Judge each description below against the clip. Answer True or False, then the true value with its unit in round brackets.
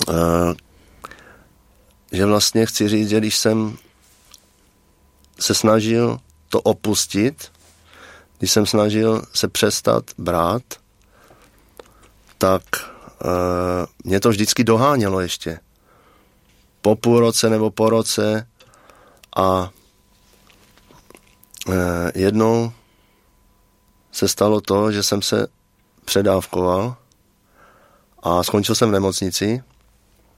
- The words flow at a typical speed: False (90 wpm)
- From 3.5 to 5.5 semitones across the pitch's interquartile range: False (2.7 semitones)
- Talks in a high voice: False (100 Hz)